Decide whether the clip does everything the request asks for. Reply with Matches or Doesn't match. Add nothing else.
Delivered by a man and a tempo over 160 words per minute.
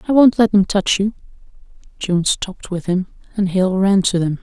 Doesn't match